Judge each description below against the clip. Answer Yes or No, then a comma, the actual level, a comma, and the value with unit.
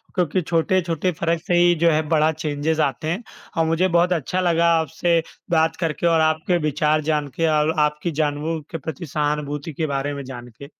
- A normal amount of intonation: No, narrow, 2.0 semitones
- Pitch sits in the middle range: Yes, medium, 160 Hz